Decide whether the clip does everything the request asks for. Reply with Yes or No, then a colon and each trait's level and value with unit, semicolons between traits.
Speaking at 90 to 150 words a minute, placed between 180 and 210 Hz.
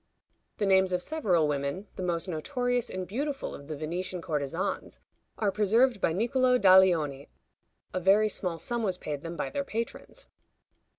No: average, 160 wpm; medium, 185 Hz